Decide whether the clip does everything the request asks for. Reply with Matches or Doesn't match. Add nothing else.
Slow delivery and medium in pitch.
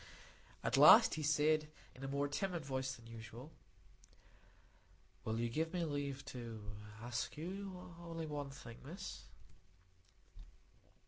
Matches